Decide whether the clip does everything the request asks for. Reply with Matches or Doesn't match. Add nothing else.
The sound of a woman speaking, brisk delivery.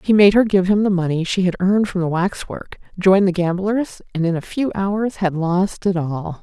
Matches